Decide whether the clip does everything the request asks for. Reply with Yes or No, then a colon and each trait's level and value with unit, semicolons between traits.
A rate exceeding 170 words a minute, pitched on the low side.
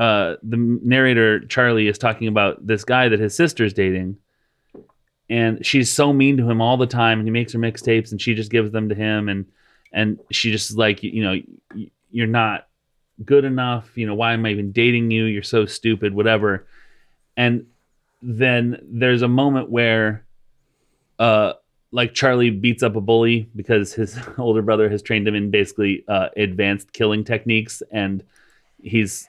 Yes: average, 180 wpm; low, 115 Hz